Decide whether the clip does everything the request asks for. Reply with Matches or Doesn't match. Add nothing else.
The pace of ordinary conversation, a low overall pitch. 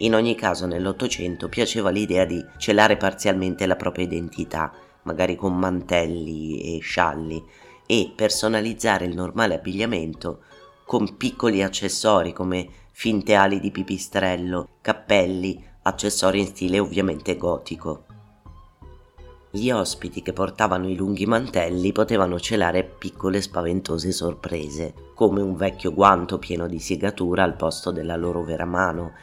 Matches